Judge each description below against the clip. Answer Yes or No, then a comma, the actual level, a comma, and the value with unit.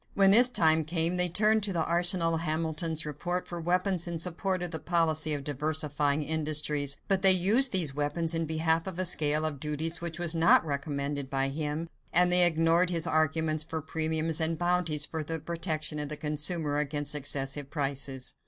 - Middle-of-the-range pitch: Yes, medium, 160 Hz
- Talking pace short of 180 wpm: No, average, 190 wpm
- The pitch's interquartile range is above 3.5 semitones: No, narrow, 2.5 semitones